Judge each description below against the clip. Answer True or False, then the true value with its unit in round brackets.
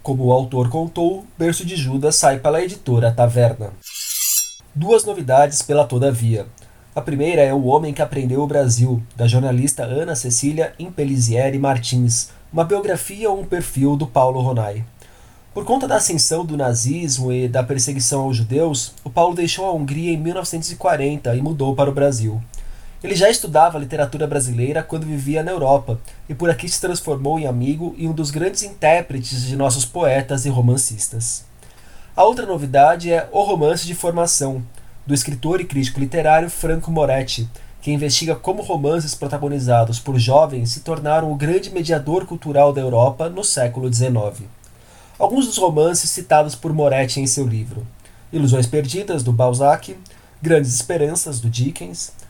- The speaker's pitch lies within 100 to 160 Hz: True (140 Hz)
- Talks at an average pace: True (160 wpm)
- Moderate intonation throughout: True (4.6 semitones)